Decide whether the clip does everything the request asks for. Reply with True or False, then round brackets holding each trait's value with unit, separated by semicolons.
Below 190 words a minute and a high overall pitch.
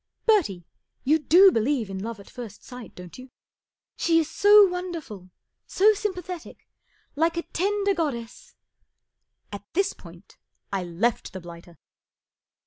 True (150 wpm; 290 Hz)